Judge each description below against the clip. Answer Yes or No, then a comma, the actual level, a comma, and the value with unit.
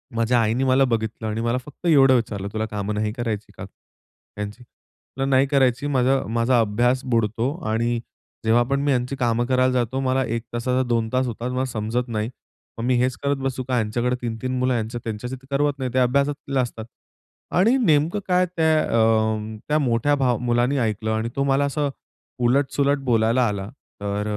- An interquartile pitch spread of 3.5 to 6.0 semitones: No, average, 3.1 semitones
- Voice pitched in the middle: No, low, 125 Hz